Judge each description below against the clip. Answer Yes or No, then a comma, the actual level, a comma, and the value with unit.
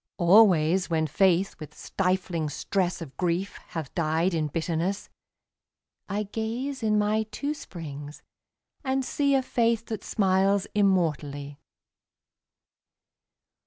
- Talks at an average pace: No, slow, 110 wpm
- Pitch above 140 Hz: Yes, medium, 185 Hz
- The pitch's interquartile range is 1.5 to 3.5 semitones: No, average, 4.7 semitones